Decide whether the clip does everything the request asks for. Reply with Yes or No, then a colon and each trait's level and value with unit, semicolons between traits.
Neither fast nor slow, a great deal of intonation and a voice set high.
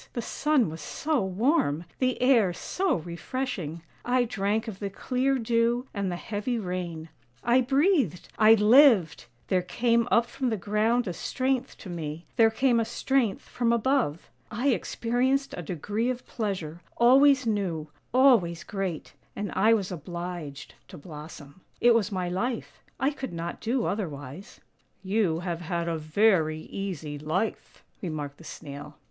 Yes: average, 155 wpm; wide, 6.2 semitones; high, 205 Hz